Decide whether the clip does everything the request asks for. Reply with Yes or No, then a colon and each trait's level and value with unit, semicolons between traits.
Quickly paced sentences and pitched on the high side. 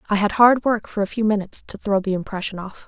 Yes: fast, 270 wpm; high, 205 Hz